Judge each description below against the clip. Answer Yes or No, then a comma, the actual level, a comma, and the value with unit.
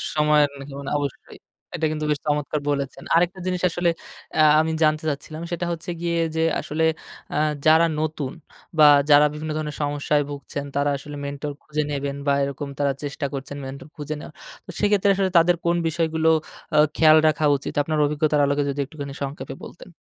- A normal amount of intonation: No, narrow, 2.1 semitones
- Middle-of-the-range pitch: Yes, medium, 150 Hz